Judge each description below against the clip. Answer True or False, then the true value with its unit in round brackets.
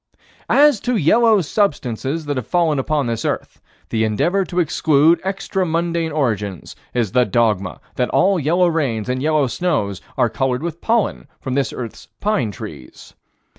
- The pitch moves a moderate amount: False (6.6 semitones)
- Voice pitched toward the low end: False (150 Hz)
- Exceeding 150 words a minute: True (160 wpm)